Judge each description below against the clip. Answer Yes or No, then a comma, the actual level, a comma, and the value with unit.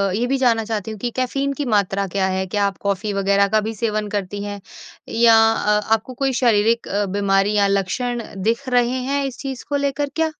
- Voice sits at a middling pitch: No, high, 215 Hz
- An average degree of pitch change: Yes, average, 3.8 semitones